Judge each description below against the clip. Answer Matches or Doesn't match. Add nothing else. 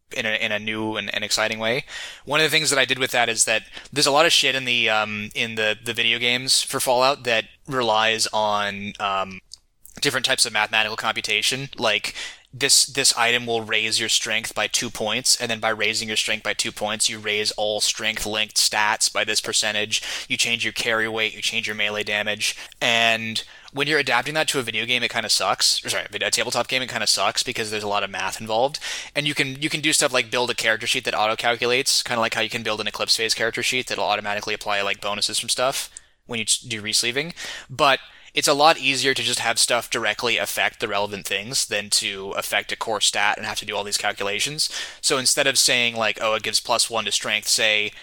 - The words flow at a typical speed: Doesn't match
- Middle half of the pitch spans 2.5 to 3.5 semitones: Matches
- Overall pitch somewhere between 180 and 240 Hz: Doesn't match